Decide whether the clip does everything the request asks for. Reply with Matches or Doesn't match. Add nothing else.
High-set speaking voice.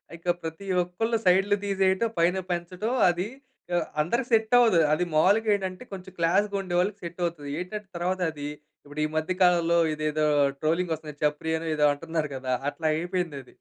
Doesn't match